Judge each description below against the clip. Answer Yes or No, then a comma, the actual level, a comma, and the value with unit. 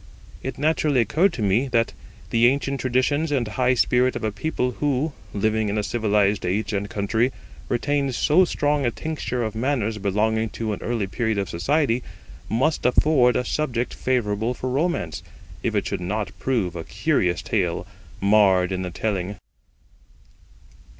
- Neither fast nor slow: Yes, average, 160 wpm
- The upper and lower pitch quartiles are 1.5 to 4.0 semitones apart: No, average, 4.5 semitones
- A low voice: Yes, low, 115 Hz